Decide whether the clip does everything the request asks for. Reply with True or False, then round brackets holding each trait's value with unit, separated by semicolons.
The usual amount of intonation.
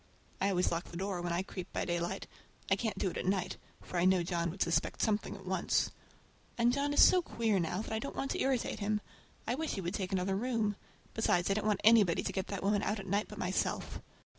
True (3.3 semitones)